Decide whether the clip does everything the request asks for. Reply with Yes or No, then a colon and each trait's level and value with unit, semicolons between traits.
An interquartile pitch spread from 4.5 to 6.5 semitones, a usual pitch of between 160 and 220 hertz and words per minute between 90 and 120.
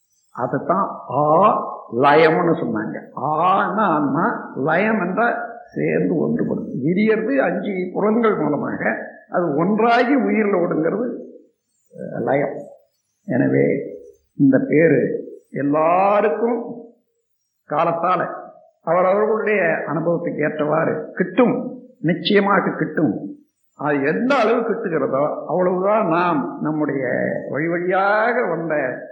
No: average, 5.1 semitones; high, 215 Hz; average, 80 wpm